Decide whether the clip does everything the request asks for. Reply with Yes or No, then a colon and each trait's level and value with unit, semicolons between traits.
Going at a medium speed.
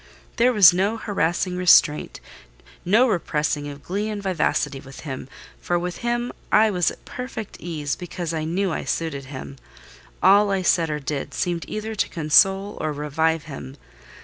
Yes: average, 165 wpm